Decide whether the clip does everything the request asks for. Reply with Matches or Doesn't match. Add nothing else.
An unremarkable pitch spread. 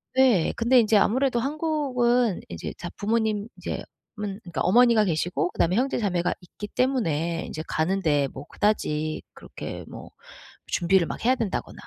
Doesn't match